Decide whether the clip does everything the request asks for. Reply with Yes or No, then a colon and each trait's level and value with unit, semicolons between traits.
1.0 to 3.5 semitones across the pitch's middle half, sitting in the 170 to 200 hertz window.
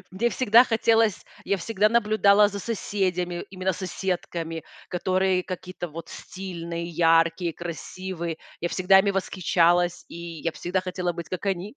Yes: narrow, 2.5 semitones; medium, 185 Hz